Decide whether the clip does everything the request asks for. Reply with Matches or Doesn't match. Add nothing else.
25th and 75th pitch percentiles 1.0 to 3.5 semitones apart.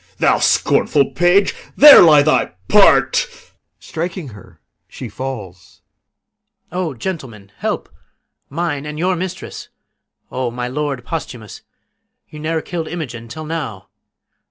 Doesn't match